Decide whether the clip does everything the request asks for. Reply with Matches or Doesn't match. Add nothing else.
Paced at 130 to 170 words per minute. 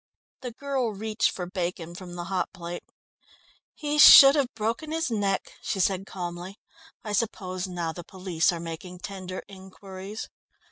Matches